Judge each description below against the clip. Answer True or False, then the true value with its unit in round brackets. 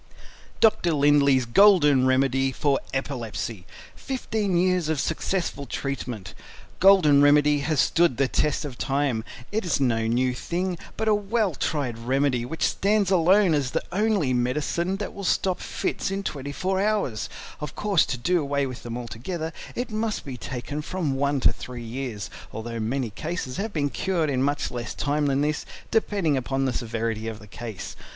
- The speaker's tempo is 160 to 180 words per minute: True (170 wpm)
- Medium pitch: True (145 Hz)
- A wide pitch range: True (6.1 semitones)